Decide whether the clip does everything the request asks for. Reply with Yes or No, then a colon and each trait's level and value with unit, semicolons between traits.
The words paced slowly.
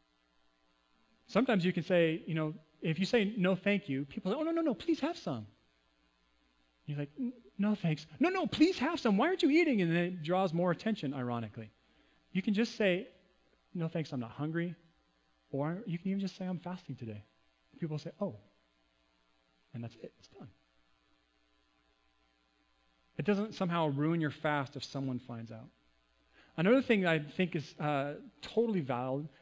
No: average, 180 wpm